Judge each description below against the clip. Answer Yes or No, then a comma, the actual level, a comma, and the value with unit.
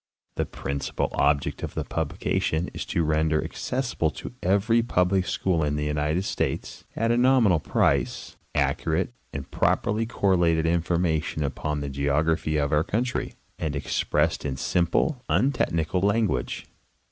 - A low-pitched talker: Yes, very low, 80 Hz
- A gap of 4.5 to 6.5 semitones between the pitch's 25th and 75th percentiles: Yes, average, 5.0 semitones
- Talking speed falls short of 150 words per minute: Yes, average, 140 wpm